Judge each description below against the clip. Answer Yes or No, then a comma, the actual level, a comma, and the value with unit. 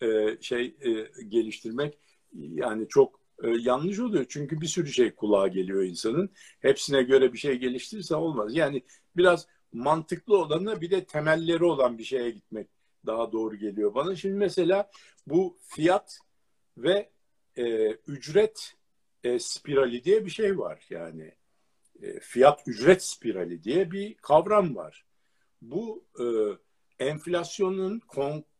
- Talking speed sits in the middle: Yes, average, 120 wpm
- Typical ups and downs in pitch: No, wide, 8.7 semitones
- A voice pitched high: No, medium, 170 Hz